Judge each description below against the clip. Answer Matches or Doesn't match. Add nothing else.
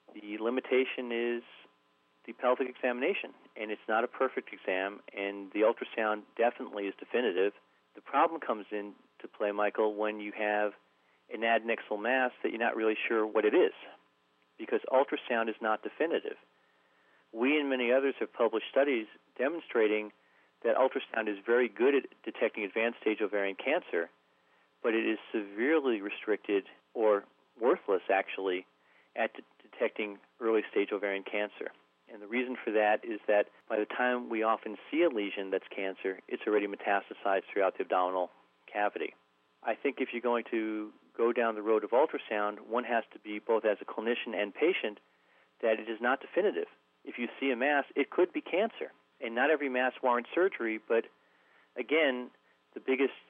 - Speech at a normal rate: Matches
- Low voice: Matches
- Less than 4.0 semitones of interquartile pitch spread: Matches